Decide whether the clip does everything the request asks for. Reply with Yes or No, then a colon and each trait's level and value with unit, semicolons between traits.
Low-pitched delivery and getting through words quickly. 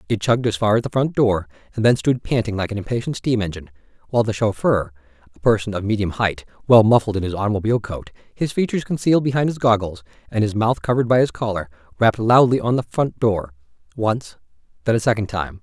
Yes: low, 110 Hz; fast, 210 wpm